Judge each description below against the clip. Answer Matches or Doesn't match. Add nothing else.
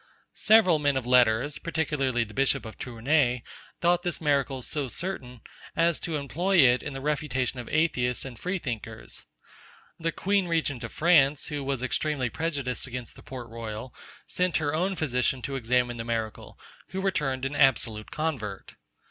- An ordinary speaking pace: Matches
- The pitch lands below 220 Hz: Matches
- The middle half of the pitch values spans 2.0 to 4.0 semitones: Doesn't match